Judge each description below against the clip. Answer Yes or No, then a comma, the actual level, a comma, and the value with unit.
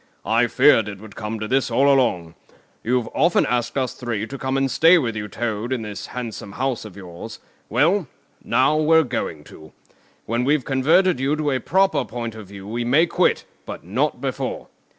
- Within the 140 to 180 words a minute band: No, average, 190 wpm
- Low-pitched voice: Yes, low, 125 Hz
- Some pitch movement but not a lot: Yes, average, 4.5 semitones